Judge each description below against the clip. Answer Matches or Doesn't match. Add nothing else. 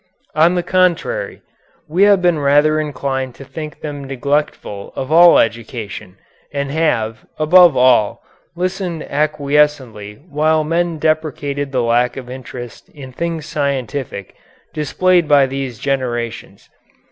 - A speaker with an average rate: Doesn't match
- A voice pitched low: Doesn't match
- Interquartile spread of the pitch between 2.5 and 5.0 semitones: Matches